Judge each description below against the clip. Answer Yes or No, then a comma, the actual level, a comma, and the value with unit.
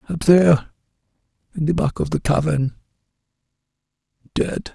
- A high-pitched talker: No, medium, 155 Hz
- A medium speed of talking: No, slow, 90 wpm